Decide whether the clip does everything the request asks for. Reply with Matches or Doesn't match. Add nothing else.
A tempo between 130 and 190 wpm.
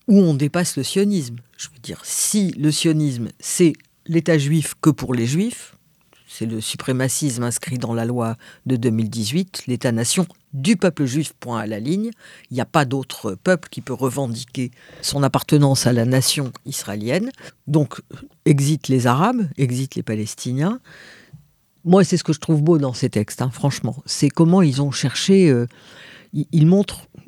Matches